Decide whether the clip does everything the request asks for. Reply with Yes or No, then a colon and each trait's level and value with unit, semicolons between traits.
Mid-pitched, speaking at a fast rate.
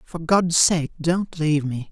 No: medium, 160 Hz; average, 190 wpm